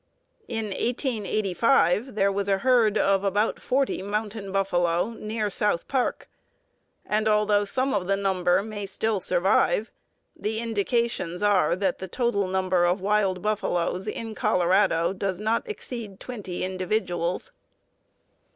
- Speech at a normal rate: No, slow, 130 wpm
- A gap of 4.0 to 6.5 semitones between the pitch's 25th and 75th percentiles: No, average, 2.7 semitones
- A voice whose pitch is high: Yes, high, 205 Hz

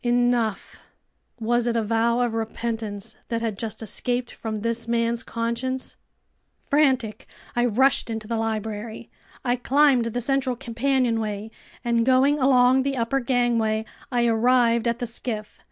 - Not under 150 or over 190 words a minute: No, average, 140 wpm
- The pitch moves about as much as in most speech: No, narrow, 1.8 semitones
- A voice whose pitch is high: Yes, high, 235 Hz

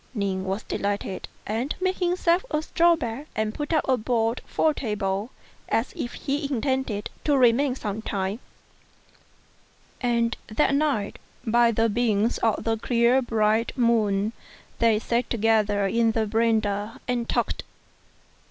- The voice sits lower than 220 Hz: No, high, 230 Hz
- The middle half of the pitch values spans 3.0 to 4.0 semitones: Yes, average, 3.3 semitones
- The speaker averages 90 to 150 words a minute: Yes, average, 145 wpm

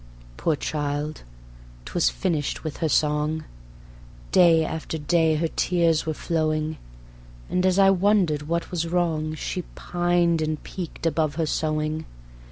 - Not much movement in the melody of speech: Yes, narrow, 1.9 semitones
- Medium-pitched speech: Yes, medium, 160 Hz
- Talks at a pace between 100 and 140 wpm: Yes, slow, 135 wpm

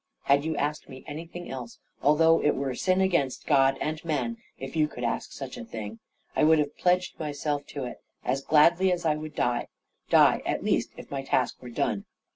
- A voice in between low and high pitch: Yes, medium, 150 Hz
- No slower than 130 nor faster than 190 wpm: No, fast, 205 wpm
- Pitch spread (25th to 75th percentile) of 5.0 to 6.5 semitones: No, average, 3.3 semitones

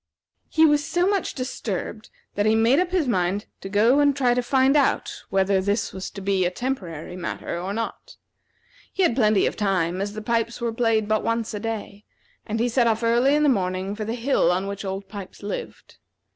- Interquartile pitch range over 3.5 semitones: Yes, average, 4.1 semitones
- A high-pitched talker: Yes, high, 220 Hz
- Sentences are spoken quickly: Yes, fast, 215 wpm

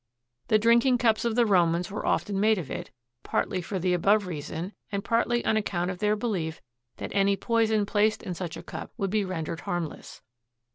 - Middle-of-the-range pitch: No, high, 200 Hz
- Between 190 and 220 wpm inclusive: Yes, average, 195 wpm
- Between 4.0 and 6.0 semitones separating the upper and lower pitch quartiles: No, average, 3.5 semitones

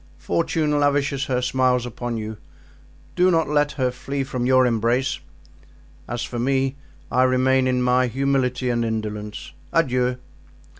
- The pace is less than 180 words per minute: Yes, average, 140 wpm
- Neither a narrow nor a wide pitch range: No, narrow, 2.0 semitones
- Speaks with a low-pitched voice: Yes, low, 130 Hz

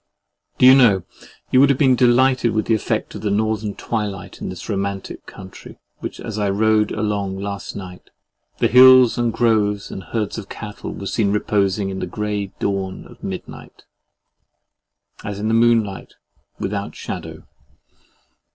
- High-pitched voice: No, low, 105 Hz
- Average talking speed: Yes, average, 155 wpm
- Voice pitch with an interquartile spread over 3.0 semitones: No, narrow, 2.6 semitones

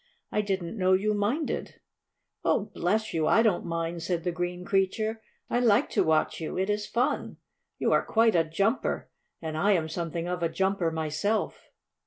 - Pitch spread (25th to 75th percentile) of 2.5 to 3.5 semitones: No, average, 4.1 semitones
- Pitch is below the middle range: No, medium, 185 Hz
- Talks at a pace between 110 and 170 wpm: No, average, 180 wpm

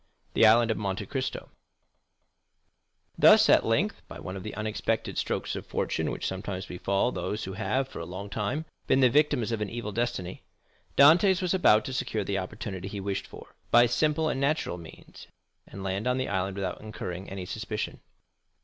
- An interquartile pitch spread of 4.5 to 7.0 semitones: Yes, average, 4.8 semitones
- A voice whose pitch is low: Yes, low, 105 Hz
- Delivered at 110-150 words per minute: No, average, 185 wpm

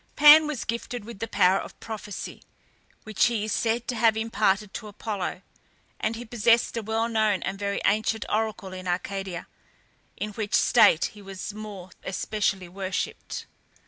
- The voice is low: No, high, 215 Hz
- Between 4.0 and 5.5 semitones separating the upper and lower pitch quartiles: No, narrow, 2.6 semitones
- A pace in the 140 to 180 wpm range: Yes, average, 160 wpm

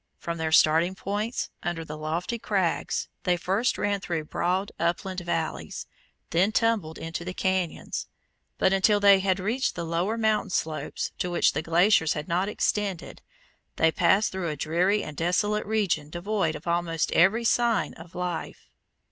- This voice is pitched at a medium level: Yes, medium, 180 Hz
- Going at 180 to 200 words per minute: No, average, 160 wpm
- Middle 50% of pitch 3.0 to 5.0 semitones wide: Yes, average, 3.8 semitones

